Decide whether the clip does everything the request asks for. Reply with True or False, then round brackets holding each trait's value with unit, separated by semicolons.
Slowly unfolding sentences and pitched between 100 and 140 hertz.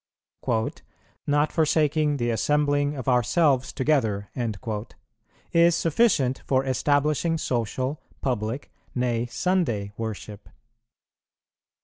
True (80 wpm; 135 Hz)